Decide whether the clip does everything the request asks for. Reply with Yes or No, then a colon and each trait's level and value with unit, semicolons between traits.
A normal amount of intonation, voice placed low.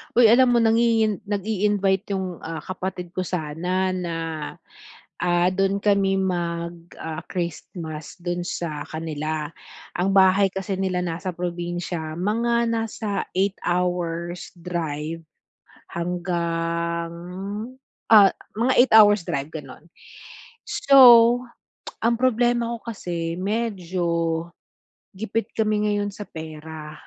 No: average, 3.7 semitones; medium, 180 Hz